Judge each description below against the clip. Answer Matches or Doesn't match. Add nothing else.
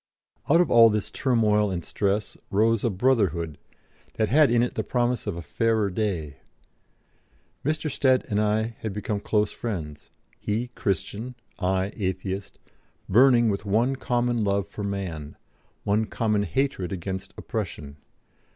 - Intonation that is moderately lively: Matches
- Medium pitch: Doesn't match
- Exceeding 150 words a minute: Doesn't match